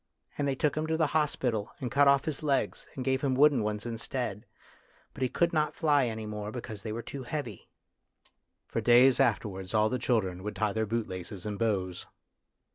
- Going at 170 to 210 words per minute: Yes, average, 200 wpm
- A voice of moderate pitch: No, low, 120 Hz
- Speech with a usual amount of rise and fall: Yes, average, 4.6 semitones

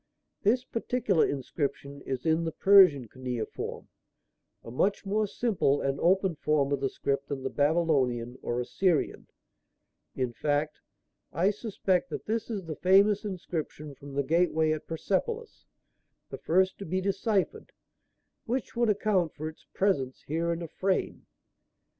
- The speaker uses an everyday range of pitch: No, wide, 5.7 semitones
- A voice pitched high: No, medium, 165 Hz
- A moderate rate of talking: Yes, average, 145 wpm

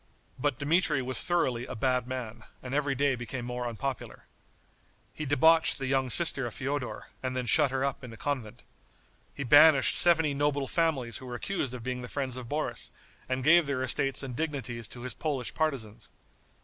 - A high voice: No, low, 130 Hz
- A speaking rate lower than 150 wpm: No, average, 190 wpm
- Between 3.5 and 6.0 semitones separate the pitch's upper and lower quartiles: No, average, 2.8 semitones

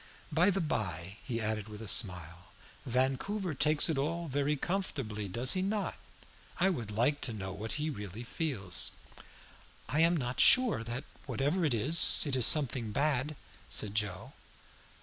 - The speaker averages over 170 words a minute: No, average, 155 wpm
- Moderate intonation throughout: No, wide, 6.7 semitones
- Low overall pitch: Yes, low, 130 Hz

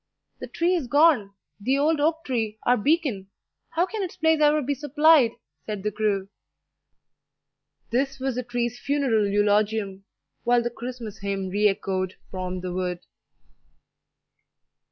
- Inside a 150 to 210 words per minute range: No, average, 140 wpm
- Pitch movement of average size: No, wide, 6.3 semitones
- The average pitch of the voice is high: Yes, high, 240 Hz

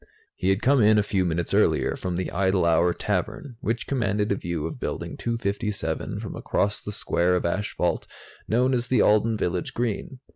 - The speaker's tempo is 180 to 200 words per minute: Yes, average, 185 wpm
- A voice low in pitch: Yes, low, 100 Hz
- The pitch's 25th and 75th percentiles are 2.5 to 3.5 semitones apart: No, average, 4.5 semitones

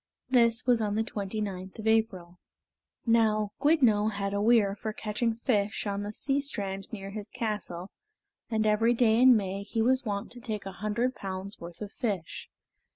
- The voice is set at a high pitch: Yes, high, 215 Hz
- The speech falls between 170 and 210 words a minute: Yes, average, 180 wpm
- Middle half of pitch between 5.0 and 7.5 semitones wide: No, narrow, 2.5 semitones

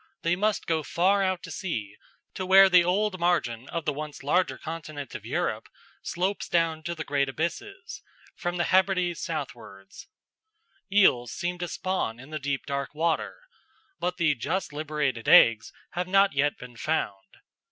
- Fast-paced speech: No, average, 165 wpm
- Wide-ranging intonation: No, average, 4.6 semitones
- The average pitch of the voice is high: No, medium, 165 Hz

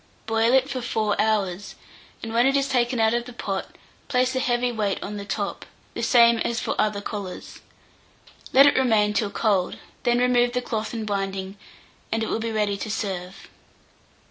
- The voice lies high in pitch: Yes, high, 225 Hz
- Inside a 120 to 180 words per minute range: No, average, 190 wpm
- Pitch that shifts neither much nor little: Yes, average, 3.0 semitones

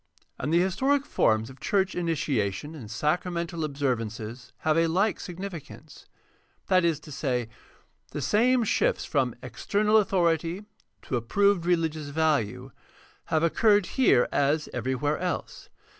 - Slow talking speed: Yes, slow, 130 wpm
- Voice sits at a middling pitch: Yes, medium, 160 Hz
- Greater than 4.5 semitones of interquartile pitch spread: Yes, average, 5.2 semitones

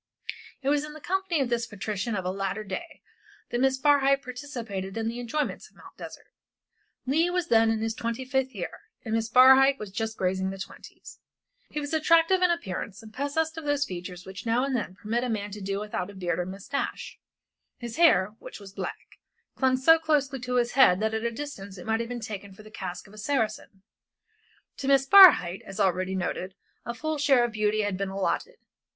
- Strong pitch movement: Yes, wide, 5.8 semitones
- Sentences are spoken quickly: Yes, fast, 210 wpm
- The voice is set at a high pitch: Yes, high, 230 Hz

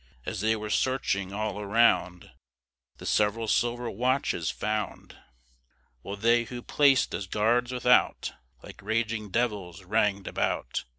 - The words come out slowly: Yes, slow, 125 wpm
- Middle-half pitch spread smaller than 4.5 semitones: Yes, average, 3.0 semitones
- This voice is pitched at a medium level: No, low, 110 Hz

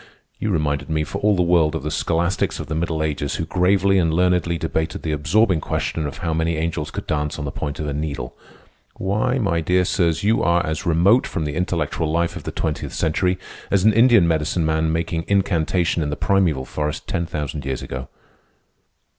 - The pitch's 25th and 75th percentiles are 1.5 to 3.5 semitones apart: Yes, average, 2.8 semitones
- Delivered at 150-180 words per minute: No, fast, 205 wpm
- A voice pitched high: No, very low, 80 Hz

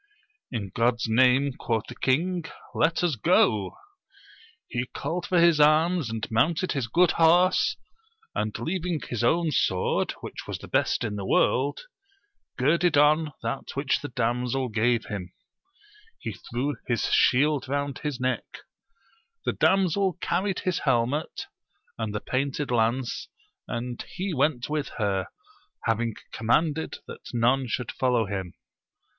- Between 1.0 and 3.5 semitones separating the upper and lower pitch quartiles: No, wide, 5.4 semitones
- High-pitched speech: No, low, 130 Hz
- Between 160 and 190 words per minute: No, average, 140 wpm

